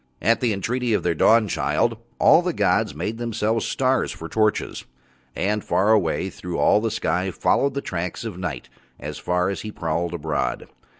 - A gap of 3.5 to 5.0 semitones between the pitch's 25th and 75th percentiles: Yes, average, 4.4 semitones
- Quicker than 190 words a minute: No, average, 175 wpm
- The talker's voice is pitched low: Yes, low, 100 Hz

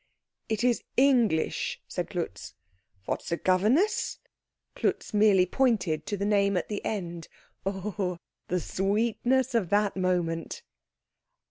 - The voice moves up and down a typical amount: Yes, average, 3.8 semitones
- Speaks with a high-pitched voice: Yes, high, 200 Hz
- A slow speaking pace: Yes, slow, 125 wpm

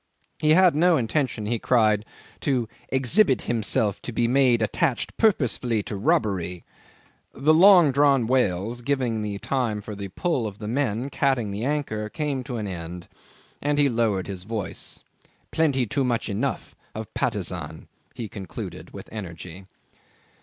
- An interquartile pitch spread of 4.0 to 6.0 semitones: Yes, average, 5.0 semitones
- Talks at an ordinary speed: Yes, average, 150 wpm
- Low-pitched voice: Yes, low, 120 Hz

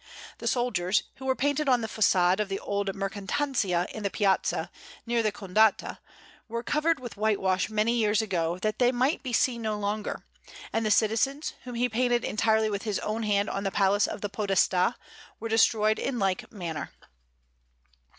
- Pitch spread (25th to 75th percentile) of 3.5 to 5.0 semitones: No, average, 3.1 semitones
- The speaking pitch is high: Yes, high, 215 Hz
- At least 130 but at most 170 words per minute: No, average, 180 wpm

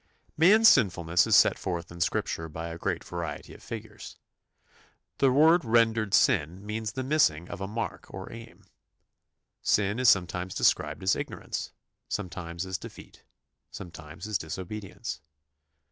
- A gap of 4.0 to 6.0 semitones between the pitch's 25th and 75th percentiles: Yes, average, 5.1 semitones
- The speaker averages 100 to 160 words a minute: Yes, average, 145 wpm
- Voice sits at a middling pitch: No, very low, 95 Hz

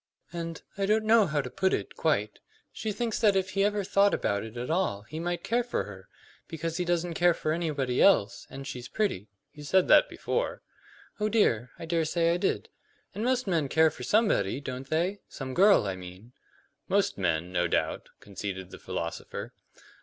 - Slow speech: No, average, 200 wpm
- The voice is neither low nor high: Yes, medium, 165 Hz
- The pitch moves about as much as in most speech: No, wide, 8.4 semitones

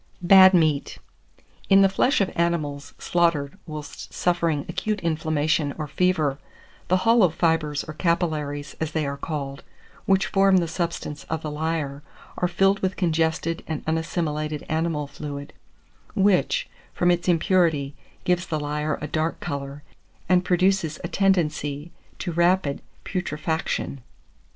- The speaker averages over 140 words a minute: No, slow, 135 wpm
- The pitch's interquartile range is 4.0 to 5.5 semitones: No, average, 3.3 semitones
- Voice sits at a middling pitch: Yes, medium, 160 Hz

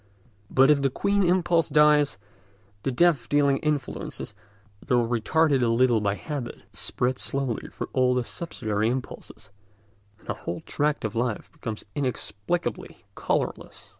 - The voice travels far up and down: No, average, 4.4 semitones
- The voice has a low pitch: Yes, low, 130 Hz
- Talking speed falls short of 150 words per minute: Yes, slow, 135 wpm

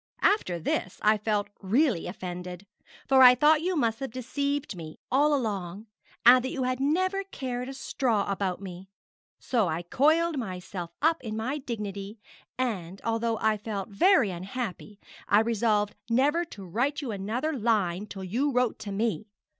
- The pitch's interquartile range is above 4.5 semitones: Yes, average, 5.2 semitones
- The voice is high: Yes, high, 225 Hz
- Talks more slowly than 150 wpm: No, average, 160 wpm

